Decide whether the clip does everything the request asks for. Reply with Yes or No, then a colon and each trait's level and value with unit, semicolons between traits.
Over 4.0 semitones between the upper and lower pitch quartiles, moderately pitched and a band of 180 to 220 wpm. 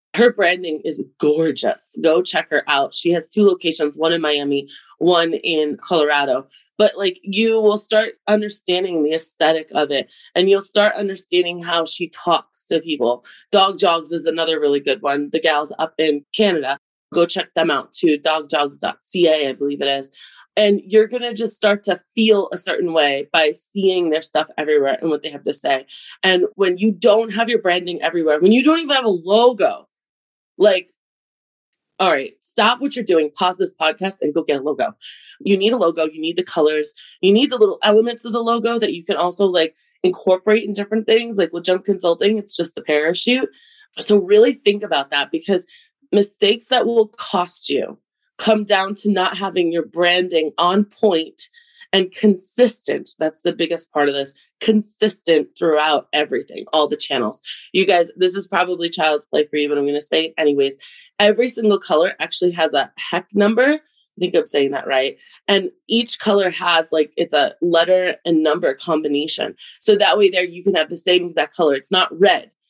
Yes: average, 4.9 semitones; medium, 180 Hz; average, 190 wpm